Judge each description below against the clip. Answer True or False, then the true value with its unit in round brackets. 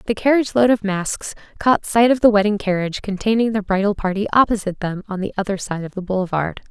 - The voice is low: False (205 Hz)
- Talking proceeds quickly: True (215 wpm)